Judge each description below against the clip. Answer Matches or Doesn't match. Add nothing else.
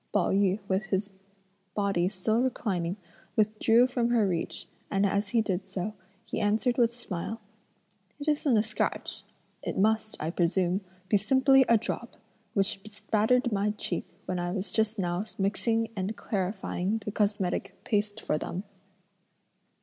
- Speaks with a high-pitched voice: Matches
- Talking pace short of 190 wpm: Matches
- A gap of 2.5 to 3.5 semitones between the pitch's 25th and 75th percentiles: Matches